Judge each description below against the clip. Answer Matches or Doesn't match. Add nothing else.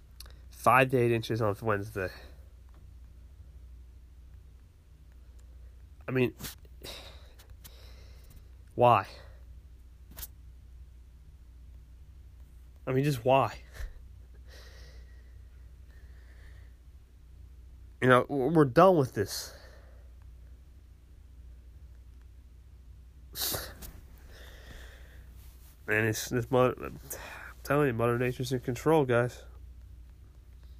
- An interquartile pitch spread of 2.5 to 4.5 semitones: Matches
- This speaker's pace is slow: Matches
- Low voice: Matches